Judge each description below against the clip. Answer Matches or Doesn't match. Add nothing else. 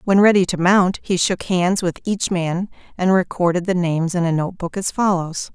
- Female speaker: Matches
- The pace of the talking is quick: Matches